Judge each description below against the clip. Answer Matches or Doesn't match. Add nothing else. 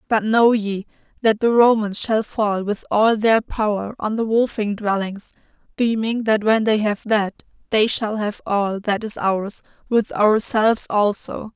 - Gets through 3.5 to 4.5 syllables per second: Matches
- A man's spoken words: Doesn't match